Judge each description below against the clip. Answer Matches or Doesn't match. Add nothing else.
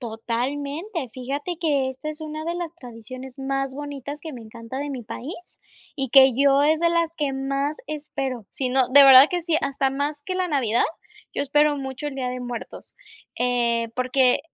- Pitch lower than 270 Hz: Doesn't match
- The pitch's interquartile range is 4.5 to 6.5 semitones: Doesn't match